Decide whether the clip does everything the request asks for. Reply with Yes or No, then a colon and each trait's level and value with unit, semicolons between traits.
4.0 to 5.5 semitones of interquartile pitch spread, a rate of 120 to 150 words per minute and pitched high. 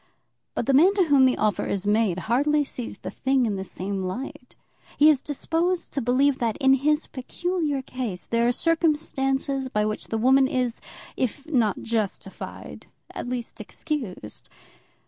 No: average, 4.4 semitones; average, 165 wpm; very high, 260 Hz